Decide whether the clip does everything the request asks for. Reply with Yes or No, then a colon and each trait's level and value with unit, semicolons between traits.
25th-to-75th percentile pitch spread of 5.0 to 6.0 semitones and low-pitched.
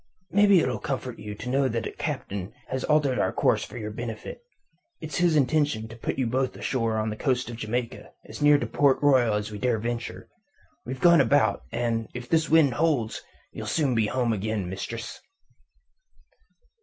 No: average, 4.3 semitones; low, 125 Hz